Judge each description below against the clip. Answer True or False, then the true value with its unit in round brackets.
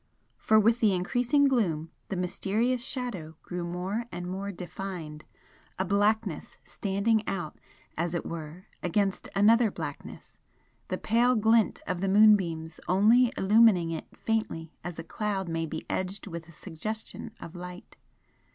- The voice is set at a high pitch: True (195 Hz)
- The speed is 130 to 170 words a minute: True (140 wpm)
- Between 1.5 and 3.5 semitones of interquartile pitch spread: False (4.2 semitones)